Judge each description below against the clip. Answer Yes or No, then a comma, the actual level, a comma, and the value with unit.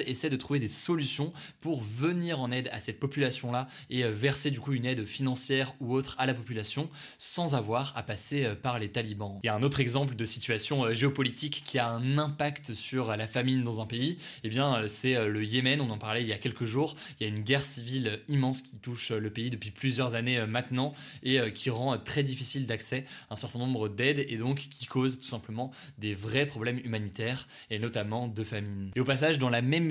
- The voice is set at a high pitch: No, low, 130 Hz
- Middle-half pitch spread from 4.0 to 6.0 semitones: No, average, 3.4 semitones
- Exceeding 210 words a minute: Yes, fast, 220 wpm